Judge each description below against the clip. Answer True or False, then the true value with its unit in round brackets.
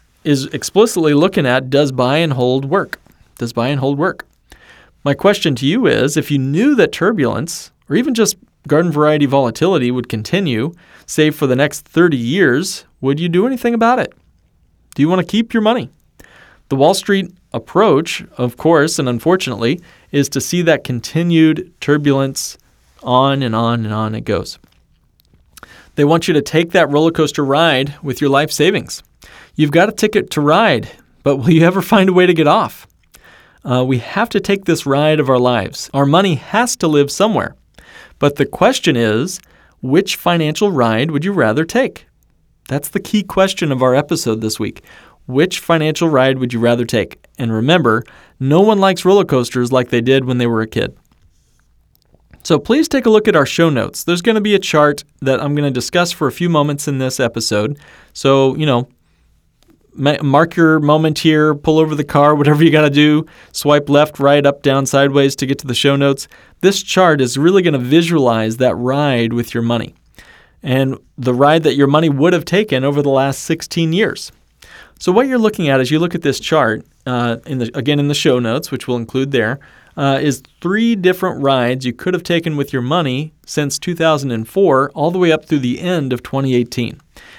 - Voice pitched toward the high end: False (145 Hz)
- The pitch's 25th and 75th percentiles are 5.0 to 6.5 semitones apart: False (4.6 semitones)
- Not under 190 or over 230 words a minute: True (195 wpm)